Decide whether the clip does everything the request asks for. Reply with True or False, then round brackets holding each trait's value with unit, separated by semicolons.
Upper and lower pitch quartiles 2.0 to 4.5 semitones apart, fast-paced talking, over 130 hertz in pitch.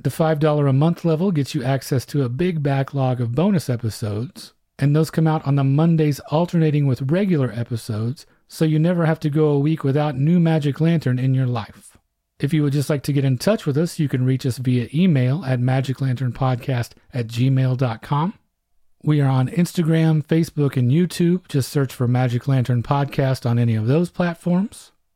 False (3.8 semitones; 190 wpm; 140 Hz)